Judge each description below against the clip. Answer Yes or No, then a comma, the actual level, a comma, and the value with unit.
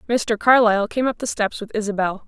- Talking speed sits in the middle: No, fast, 210 wpm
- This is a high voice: Yes, high, 215 Hz